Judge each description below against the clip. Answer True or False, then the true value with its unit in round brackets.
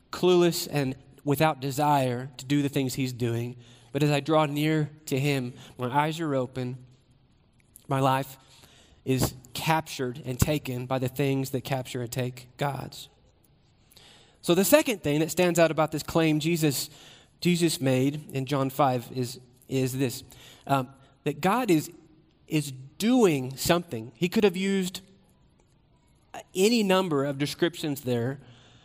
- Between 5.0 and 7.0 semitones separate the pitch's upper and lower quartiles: False (3.5 semitones)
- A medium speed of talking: True (145 wpm)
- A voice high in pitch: False (140 Hz)